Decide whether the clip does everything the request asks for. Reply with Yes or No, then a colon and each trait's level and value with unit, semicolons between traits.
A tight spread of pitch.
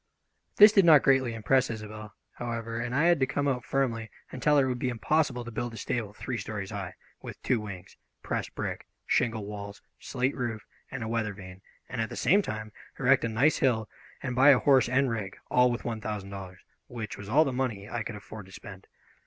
No: average, 3.5 semitones